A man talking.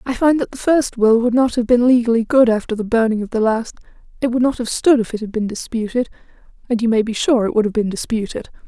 No: female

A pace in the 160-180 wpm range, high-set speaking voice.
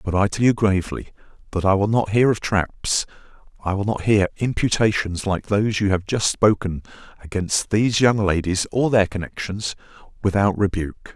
No: average, 165 wpm; low, 100 Hz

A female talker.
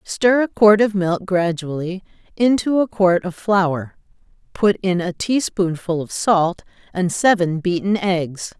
Yes: female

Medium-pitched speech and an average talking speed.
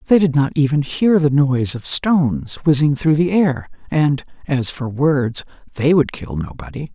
Yes: medium, 145 Hz; average, 180 wpm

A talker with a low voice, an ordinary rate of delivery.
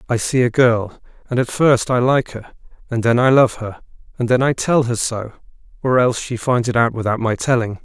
No: low, 120 Hz; fast, 215 wpm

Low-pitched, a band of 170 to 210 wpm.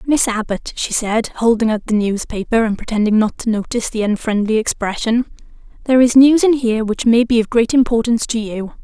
No: high, 225 Hz; average, 195 wpm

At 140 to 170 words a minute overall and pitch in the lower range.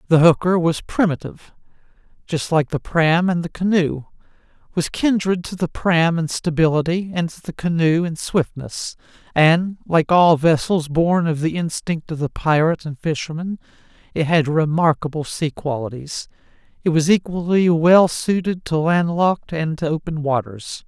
No: average, 150 wpm; medium, 165 Hz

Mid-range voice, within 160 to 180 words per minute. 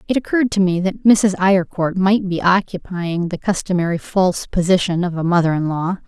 No: medium, 180 Hz; average, 190 wpm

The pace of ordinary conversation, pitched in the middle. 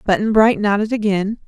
No: average, 160 wpm; high, 210 Hz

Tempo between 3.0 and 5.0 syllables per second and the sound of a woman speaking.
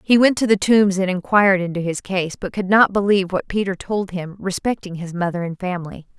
No: 5.7 syllables/s; female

